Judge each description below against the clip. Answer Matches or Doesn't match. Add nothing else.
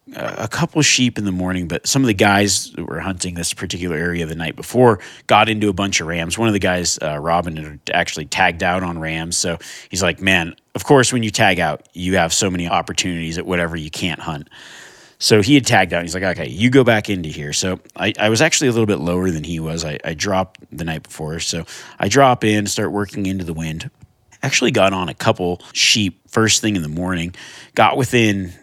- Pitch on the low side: Matches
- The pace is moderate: Doesn't match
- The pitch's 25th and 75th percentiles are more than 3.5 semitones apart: Matches